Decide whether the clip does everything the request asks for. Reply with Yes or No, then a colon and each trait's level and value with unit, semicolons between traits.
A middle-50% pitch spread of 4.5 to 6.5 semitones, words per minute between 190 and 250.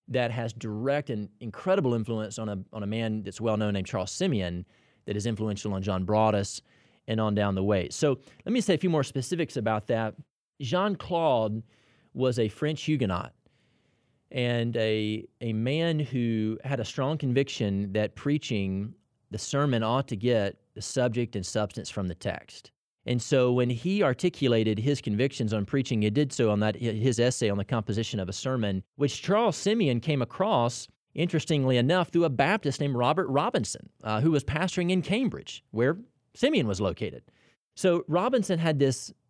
No: average, 5.1 semitones; average, 175 wpm